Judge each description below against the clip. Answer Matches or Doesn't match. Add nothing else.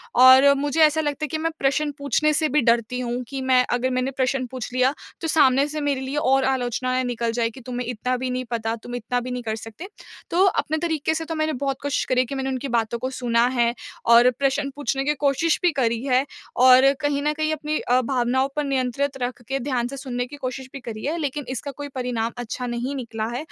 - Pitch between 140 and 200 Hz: Doesn't match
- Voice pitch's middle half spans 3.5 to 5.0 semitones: Doesn't match